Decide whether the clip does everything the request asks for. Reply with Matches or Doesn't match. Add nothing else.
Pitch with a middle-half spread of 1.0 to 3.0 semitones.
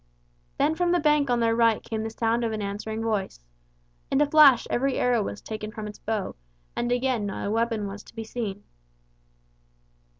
Matches